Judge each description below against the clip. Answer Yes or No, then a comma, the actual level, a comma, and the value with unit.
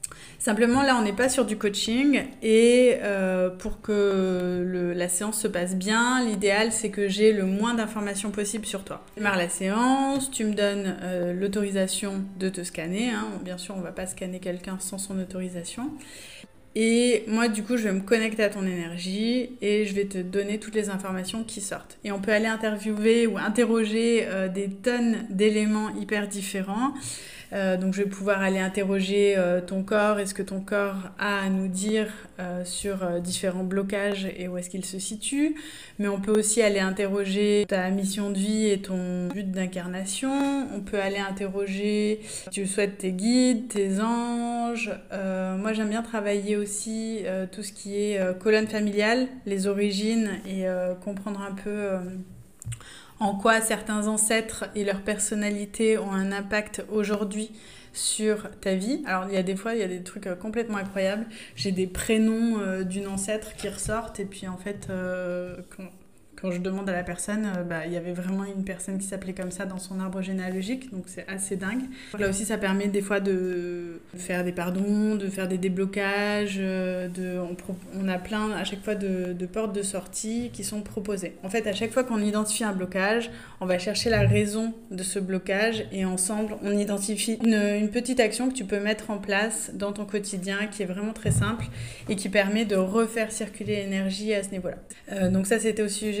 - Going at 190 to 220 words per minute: Yes, average, 195 wpm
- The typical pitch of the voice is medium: No, high, 200 Hz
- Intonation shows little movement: Yes, narrow, 2.3 semitones